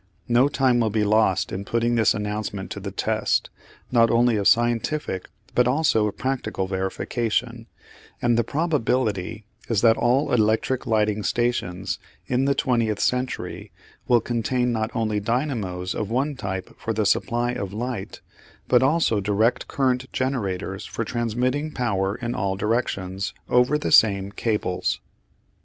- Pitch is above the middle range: No, low, 115 Hz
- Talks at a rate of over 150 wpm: No, average, 145 wpm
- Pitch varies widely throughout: No, average, 3.3 semitones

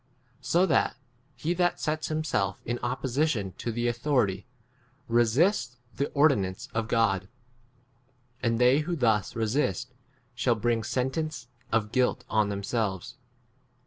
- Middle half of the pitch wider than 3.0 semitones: Yes, average, 4.2 semitones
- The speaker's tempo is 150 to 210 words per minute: No, slow, 135 wpm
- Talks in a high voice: No, low, 120 Hz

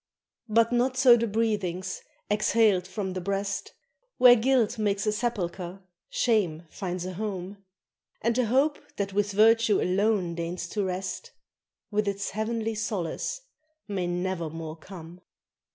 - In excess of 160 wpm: No, slow, 135 wpm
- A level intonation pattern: No, average, 3.6 semitones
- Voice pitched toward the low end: No, high, 200 Hz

